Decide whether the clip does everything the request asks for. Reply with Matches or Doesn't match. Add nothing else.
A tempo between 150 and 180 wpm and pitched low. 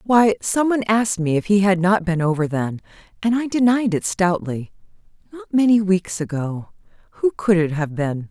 Doesn't match